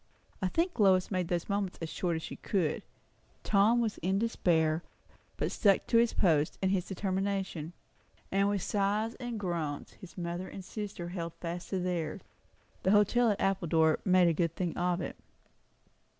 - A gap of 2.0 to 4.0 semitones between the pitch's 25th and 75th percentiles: Yes, average, 2.8 semitones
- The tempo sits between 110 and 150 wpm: No, average, 170 wpm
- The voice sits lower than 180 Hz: No, medium, 185 Hz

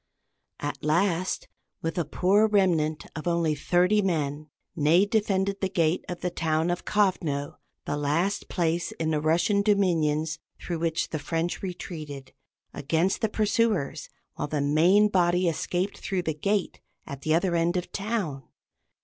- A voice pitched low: No, medium, 170 Hz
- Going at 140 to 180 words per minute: Yes, average, 155 wpm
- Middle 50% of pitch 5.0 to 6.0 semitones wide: No, average, 3.6 semitones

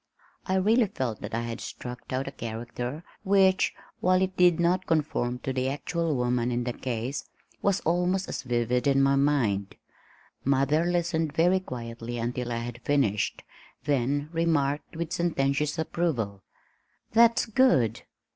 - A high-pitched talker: No, medium, 140 Hz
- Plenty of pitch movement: Yes, wide, 6.0 semitones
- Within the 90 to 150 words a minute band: Yes, average, 145 wpm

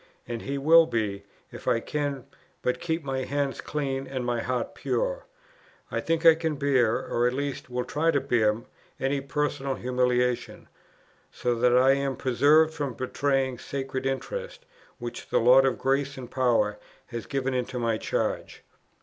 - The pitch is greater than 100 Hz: Yes, low, 135 Hz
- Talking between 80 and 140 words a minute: No, average, 165 wpm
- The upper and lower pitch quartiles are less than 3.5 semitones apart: Yes, narrow, 2.5 semitones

